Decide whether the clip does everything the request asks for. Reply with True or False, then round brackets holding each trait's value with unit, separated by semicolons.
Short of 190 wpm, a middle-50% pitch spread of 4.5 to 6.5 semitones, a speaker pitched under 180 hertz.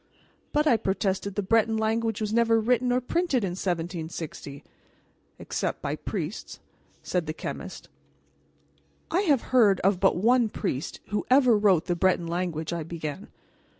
False (150 wpm; 5.0 semitones; 200 Hz)